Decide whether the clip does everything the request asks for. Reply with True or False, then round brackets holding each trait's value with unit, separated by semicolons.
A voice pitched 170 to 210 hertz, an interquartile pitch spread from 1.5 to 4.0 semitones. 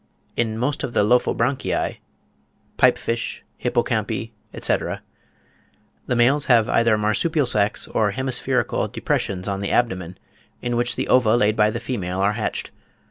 False (115 Hz; 3.0 semitones)